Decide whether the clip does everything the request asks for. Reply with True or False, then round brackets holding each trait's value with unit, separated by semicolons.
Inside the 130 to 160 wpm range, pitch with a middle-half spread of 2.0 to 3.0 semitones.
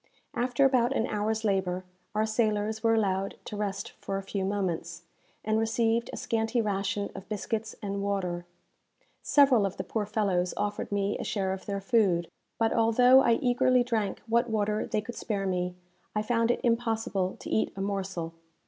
False (175 wpm; 2.7 semitones)